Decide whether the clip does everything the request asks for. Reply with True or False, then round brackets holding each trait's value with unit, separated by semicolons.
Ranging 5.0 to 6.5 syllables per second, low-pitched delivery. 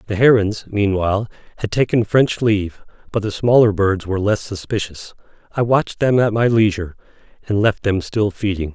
True (5.4 syllables/s; 105 Hz)